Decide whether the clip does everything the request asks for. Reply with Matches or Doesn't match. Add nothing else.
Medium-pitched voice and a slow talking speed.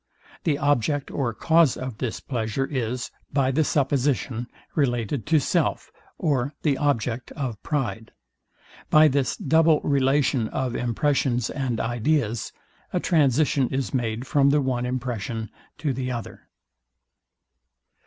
Doesn't match